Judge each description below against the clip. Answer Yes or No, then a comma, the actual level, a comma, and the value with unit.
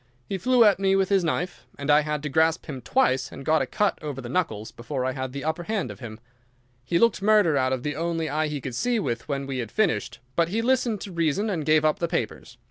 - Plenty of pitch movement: Yes, wide, 6.2 semitones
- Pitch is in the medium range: Yes, medium, 155 Hz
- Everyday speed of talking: No, fast, 260 wpm